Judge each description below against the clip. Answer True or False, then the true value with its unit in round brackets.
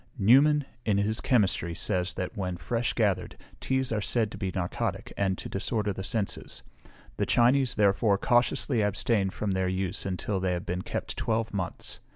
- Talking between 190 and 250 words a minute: False (175 wpm)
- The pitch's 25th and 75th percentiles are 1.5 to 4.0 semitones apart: True (3.6 semitones)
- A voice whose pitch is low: True (100 Hz)